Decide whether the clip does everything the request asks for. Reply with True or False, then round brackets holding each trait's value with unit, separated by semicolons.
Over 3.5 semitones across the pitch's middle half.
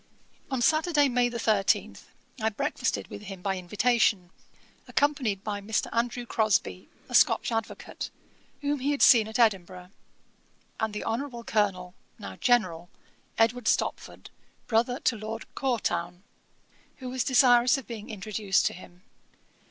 True (4.0 semitones)